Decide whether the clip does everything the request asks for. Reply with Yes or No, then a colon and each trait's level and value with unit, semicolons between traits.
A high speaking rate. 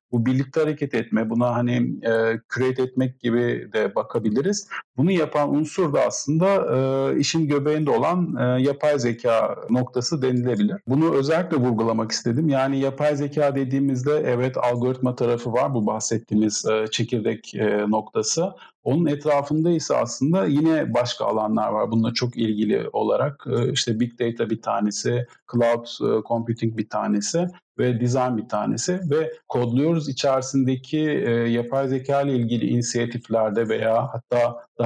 Yes: fast, 145 wpm